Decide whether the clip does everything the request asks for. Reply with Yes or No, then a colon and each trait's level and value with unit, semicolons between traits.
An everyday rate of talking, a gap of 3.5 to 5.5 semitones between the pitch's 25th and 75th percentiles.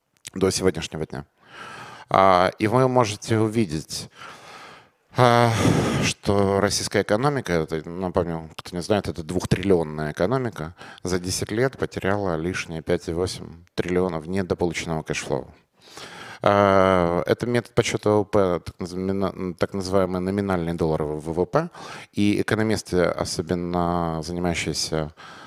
No: slow, 95 wpm; average, 3.8 semitones